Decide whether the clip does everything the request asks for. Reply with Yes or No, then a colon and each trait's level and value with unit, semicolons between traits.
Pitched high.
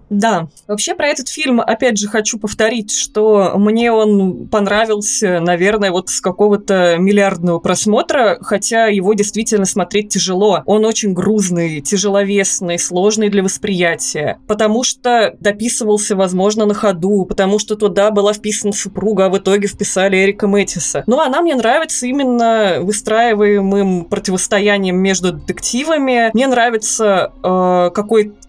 Yes: high, 205 Hz